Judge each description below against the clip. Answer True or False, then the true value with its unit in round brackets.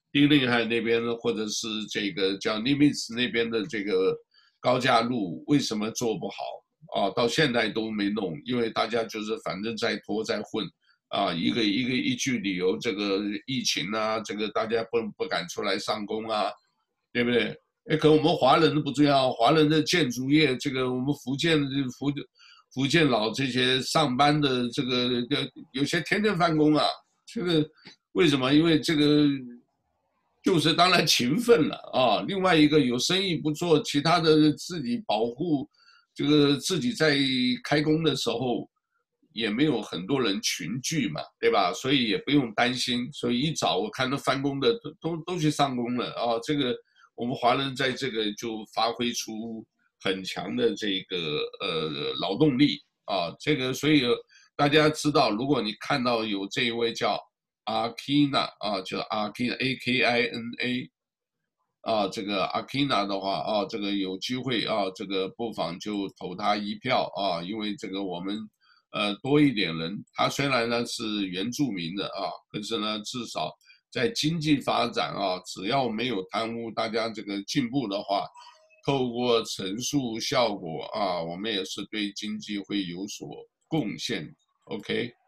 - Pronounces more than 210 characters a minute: True (240 characters per minute)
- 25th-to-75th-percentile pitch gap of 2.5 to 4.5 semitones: False (5.3 semitones)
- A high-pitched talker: False (125 Hz)